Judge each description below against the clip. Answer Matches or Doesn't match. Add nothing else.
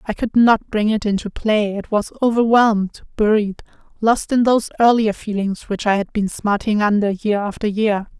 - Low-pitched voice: Doesn't match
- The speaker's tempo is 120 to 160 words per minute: Doesn't match